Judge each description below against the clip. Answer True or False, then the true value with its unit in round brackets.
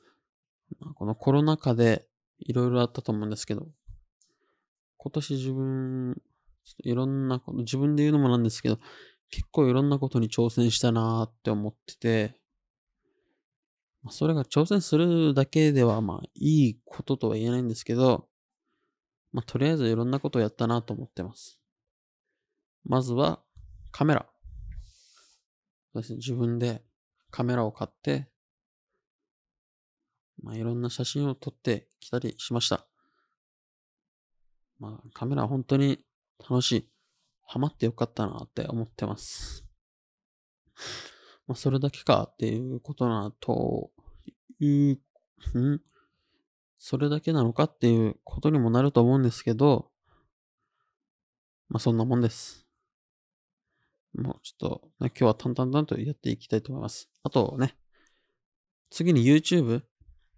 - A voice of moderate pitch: False (125 Hz)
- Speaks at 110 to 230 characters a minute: False (265 characters per minute)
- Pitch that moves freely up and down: False (3.9 semitones)